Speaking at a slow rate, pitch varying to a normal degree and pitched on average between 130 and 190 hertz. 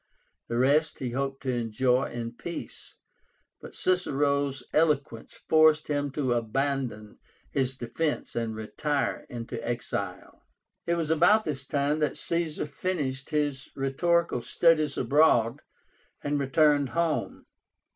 Yes: slow, 120 wpm; average, 3.8 semitones; medium, 140 Hz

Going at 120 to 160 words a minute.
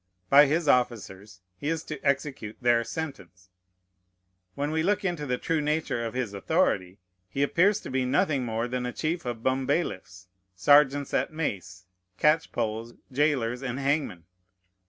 Yes: average, 150 wpm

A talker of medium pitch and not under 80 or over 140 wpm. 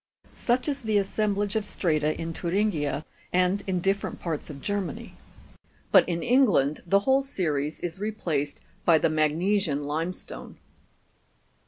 Yes: medium, 180 Hz; slow, 135 wpm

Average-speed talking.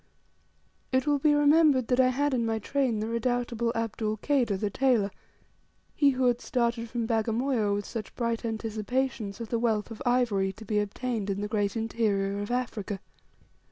Yes: average, 170 wpm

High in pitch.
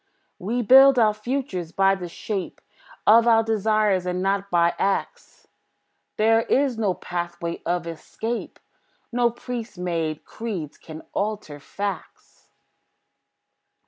Yes: high, 200 Hz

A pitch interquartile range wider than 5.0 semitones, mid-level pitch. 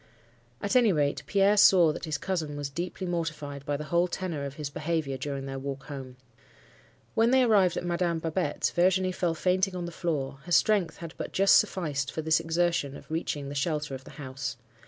No: average, 4.1 semitones; medium, 160 Hz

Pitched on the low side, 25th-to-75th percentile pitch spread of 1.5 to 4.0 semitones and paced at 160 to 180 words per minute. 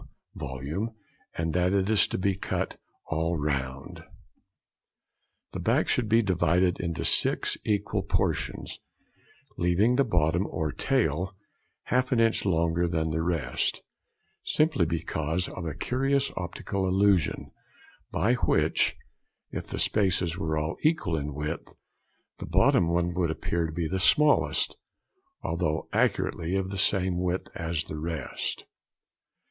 No: very low, 90 Hz; average, 3.4 semitones; slow, 135 wpm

